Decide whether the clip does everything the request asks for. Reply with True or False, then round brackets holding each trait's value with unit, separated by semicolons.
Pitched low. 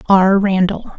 False (190 Hz)